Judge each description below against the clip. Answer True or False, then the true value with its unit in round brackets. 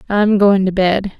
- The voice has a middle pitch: False (195 Hz)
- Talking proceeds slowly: False (200 wpm)